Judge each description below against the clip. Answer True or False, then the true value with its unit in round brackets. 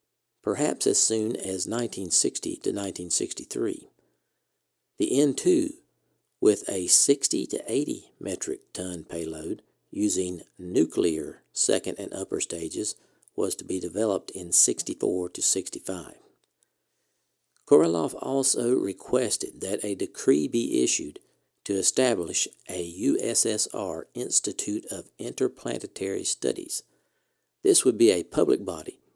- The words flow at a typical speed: False (110 wpm)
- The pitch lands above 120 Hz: True (135 Hz)